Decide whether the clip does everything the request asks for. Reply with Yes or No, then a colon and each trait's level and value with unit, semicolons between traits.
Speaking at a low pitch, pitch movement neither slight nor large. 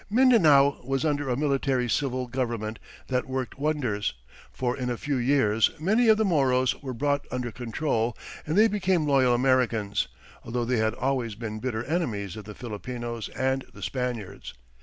Yes: low, 130 Hz; average, 3.5 semitones